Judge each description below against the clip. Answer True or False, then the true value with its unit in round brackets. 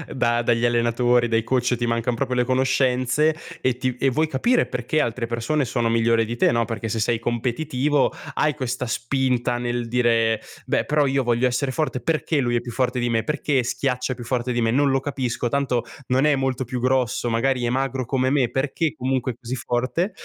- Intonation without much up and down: True (2.0 semitones)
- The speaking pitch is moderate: False (125 Hz)